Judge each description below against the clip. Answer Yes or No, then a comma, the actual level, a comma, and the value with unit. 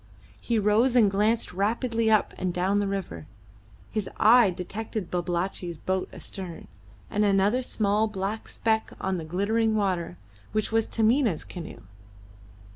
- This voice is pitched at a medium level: No, high, 205 Hz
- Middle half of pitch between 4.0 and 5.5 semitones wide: No, average, 3.1 semitones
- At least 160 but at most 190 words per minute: No, slow, 135 wpm